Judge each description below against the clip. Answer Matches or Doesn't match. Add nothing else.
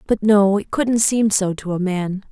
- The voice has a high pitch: Matches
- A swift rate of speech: Matches